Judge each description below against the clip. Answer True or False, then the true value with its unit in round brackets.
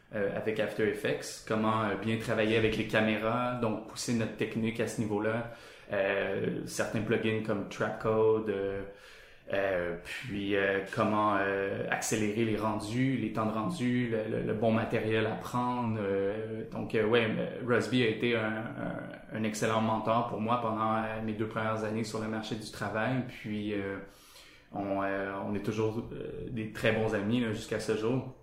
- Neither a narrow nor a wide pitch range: False (0.9 semitones)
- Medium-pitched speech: False (110 Hz)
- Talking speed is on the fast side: False (175 wpm)